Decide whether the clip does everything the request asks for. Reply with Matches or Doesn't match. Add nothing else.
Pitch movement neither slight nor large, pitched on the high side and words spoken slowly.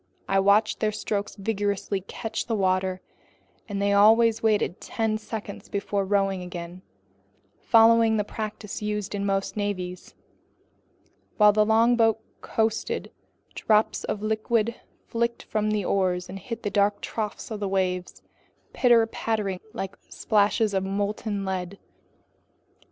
Doesn't match